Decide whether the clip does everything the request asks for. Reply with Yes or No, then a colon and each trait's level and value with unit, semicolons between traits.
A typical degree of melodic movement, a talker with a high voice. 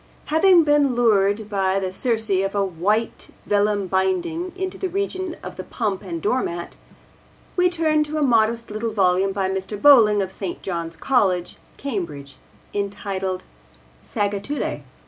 No: wide, 6.1 semitones; high, 205 Hz